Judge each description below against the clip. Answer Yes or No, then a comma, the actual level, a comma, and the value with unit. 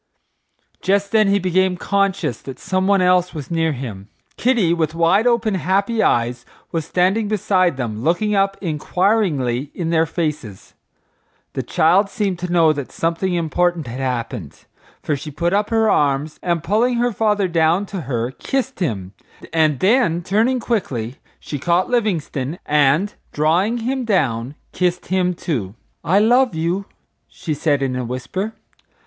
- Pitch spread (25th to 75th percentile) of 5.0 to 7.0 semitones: Yes, wide, 5.4 semitones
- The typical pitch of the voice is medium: Yes, medium, 175 Hz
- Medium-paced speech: Yes, average, 155 wpm